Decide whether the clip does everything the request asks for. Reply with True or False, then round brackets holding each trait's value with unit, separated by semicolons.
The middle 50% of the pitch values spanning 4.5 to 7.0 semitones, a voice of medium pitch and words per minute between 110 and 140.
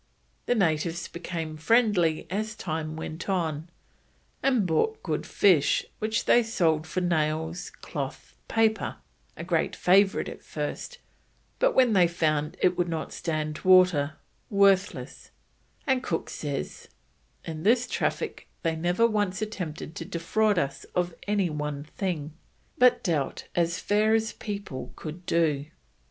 True (4.8 semitones; 175 Hz; 135 wpm)